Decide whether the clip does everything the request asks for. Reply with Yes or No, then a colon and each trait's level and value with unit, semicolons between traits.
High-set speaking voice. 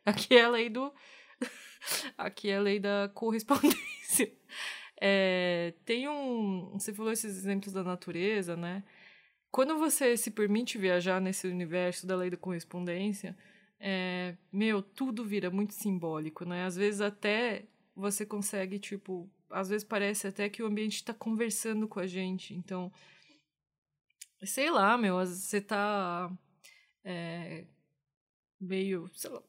Yes: high, 200 Hz